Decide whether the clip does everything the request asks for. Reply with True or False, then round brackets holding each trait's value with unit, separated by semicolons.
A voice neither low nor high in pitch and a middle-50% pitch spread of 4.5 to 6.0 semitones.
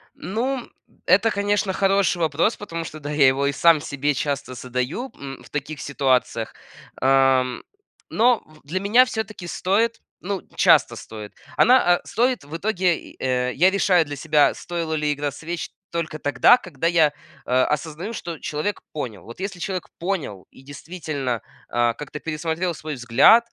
True (160 Hz; 5.2 semitones)